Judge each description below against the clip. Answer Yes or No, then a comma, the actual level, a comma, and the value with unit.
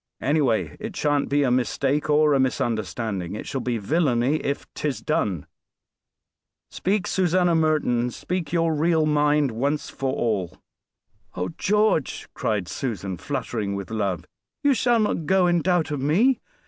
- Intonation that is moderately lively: No, wide, 5.9 semitones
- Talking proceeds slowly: No, average, 150 wpm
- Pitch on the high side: No, medium, 145 Hz